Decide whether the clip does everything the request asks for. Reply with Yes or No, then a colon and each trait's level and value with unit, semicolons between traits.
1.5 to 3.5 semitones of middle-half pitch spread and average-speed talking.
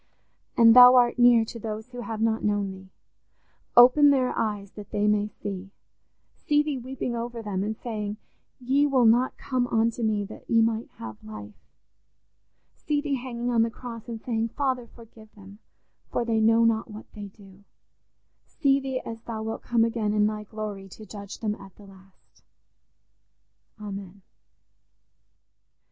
Yes: average, 2.7 semitones; average, 160 wpm